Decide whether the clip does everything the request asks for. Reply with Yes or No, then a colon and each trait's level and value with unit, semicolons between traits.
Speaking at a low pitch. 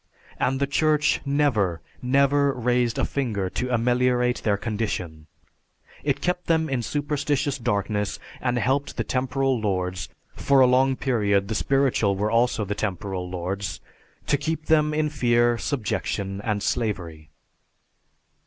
Yes: low, 120 Hz